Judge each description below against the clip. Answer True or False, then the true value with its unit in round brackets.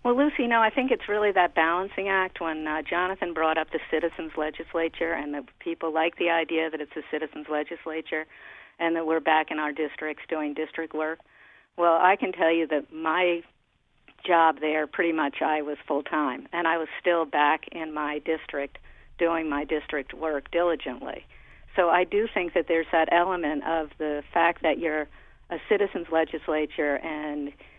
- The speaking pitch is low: False (160 Hz)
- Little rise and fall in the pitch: True (1.8 semitones)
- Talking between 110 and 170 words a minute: False (180 wpm)